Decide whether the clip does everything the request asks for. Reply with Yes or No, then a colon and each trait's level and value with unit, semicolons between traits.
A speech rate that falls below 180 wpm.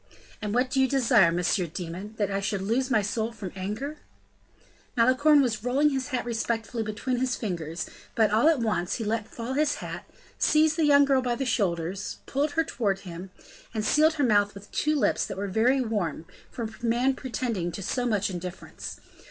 No: average, 195 wpm